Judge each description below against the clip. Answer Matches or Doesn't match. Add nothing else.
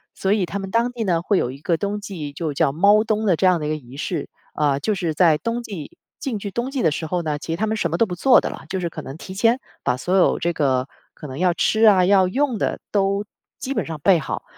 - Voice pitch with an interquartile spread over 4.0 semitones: Matches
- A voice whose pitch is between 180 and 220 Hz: Matches